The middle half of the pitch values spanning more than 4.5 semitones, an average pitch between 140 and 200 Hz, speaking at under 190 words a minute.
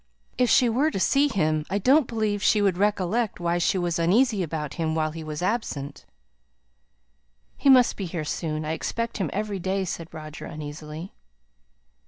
Yes: wide, 5.4 semitones; medium, 185 Hz; average, 175 wpm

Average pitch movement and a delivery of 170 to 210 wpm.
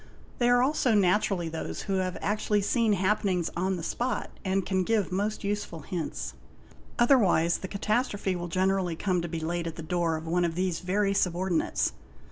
Yes: average, 3.1 semitones; average, 185 wpm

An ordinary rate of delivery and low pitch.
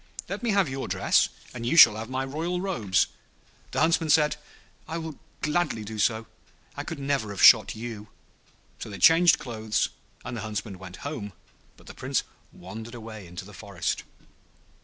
Yes: average, 175 wpm; low, 115 Hz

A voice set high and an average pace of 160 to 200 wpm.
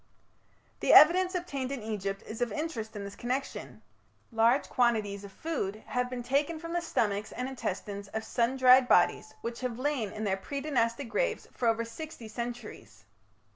Yes: high, 240 Hz; average, 175 wpm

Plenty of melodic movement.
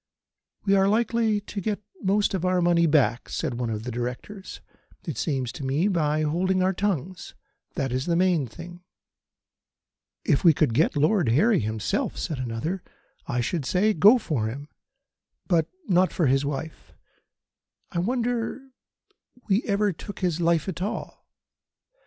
Yes: wide, 5.9 semitones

